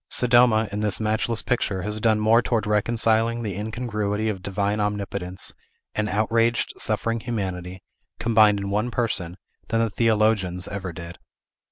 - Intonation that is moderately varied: No, narrow, 2.3 semitones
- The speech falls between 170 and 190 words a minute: No, average, 145 wpm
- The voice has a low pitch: Yes, low, 105 Hz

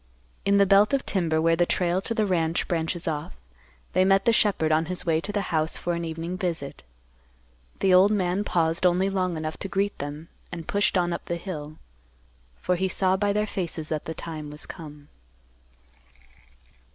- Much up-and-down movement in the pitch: No, average, 3.2 semitones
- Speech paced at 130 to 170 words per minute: No, average, 190 wpm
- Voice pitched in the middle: Yes, medium, 175 Hz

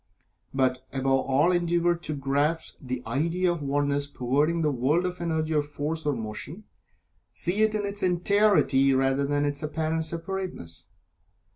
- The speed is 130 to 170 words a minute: Yes, average, 160 wpm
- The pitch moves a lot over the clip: No, average, 4.1 semitones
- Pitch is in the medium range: Yes, medium, 150 Hz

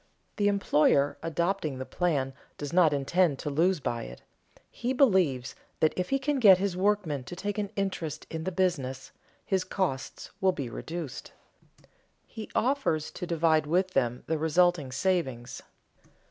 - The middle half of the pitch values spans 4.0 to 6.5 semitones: Yes, average, 5.0 semitones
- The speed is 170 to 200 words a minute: No, average, 160 wpm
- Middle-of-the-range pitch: Yes, medium, 170 Hz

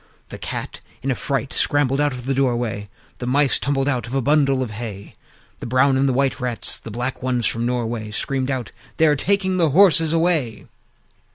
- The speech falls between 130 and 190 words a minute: No, average, 200 wpm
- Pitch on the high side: No, low, 130 Hz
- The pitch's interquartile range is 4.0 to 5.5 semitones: No, average, 3.0 semitones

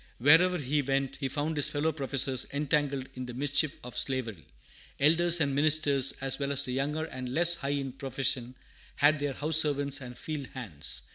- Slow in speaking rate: No, average, 185 wpm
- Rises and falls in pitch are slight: Yes, narrow, 2.3 semitones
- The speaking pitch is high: No, medium, 140 Hz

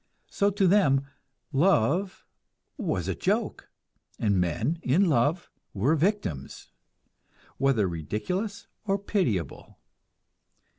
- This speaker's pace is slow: Yes, slow, 95 wpm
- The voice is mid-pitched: Yes, medium, 145 Hz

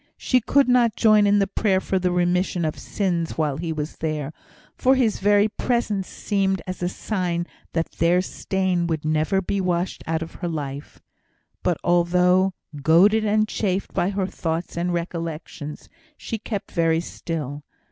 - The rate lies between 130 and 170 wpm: Yes, average, 165 wpm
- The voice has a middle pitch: Yes, medium, 180 Hz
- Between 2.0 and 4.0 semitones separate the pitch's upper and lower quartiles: Yes, average, 3.4 semitones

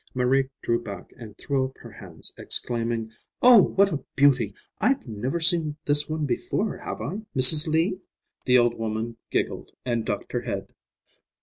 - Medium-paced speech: Yes, average, 165 wpm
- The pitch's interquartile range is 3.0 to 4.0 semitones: No, average, 5.0 semitones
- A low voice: Yes, low, 130 Hz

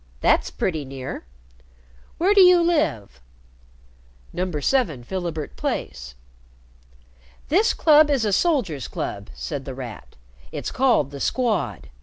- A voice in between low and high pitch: Yes, medium, 180 Hz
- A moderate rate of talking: No, slow, 120 wpm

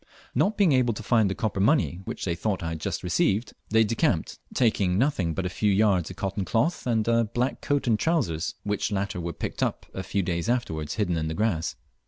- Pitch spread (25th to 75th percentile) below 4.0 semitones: No, average, 4.6 semitones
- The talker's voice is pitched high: No, low, 105 Hz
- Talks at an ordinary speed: No, fast, 225 wpm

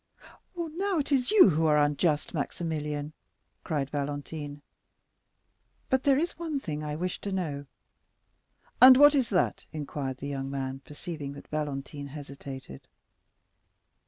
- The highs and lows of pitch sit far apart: Yes, wide, 6.1 semitones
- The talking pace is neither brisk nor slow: No, slow, 130 wpm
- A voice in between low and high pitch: Yes, medium, 150 Hz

